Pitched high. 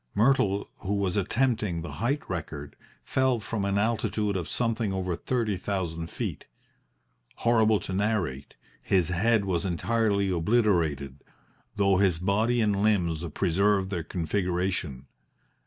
No: low, 100 Hz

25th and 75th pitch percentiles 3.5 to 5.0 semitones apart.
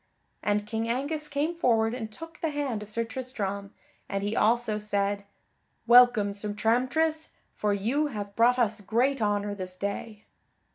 Yes: average, 3.8 semitones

